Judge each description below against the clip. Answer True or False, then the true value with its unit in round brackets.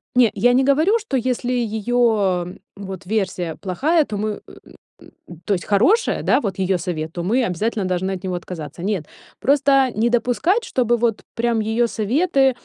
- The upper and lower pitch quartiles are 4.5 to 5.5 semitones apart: True (5.1 semitones)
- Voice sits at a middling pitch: False (220 Hz)